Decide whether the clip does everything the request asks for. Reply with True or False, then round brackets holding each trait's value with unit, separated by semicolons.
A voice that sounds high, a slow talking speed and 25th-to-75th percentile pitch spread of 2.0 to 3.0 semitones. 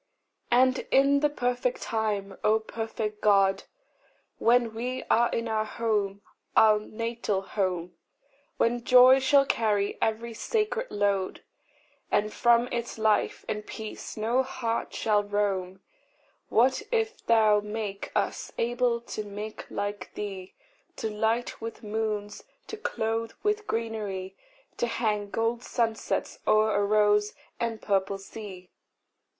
True (220 Hz; 125 wpm; 2.4 semitones)